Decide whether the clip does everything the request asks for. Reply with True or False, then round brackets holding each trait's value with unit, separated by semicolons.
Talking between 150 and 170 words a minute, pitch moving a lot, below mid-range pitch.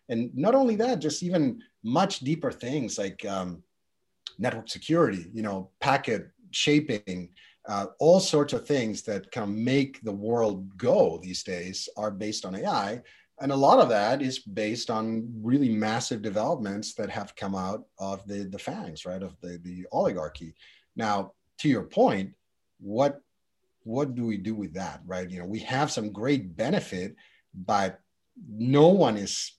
True (165 wpm; 6.3 semitones; 110 Hz)